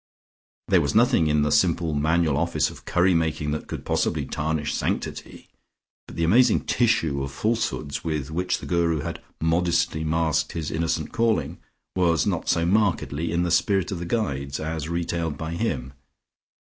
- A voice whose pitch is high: No, very low, 80 Hz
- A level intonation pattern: Yes, narrow, 2.2 semitones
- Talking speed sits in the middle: Yes, average, 165 wpm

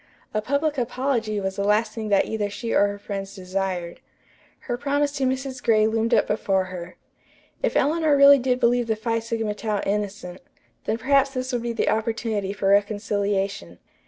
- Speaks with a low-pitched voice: No, high, 220 Hz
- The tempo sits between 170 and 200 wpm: Yes, average, 180 wpm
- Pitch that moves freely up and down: No, average, 3.8 semitones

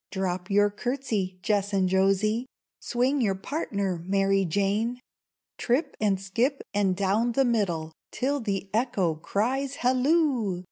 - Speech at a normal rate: No, slow, 130 wpm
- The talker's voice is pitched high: Yes, high, 205 Hz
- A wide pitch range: No, average, 4.3 semitones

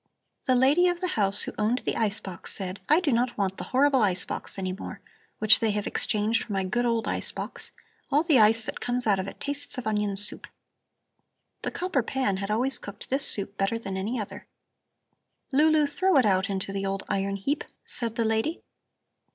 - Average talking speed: No, fast, 210 wpm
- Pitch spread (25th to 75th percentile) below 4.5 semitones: No, average, 5.1 semitones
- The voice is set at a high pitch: Yes, high, 220 Hz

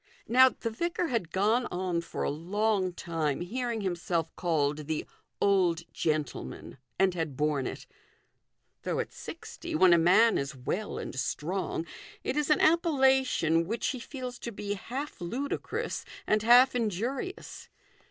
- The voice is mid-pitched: No, high, 195 Hz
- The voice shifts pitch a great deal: Yes, wide, 6.9 semitones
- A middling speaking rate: Yes, average, 150 wpm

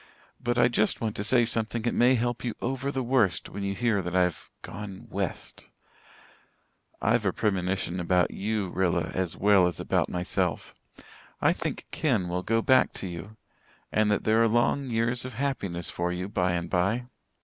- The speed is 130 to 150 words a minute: No, average, 180 wpm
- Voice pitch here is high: No, low, 105 Hz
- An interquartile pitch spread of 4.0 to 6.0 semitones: Yes, average, 4.7 semitones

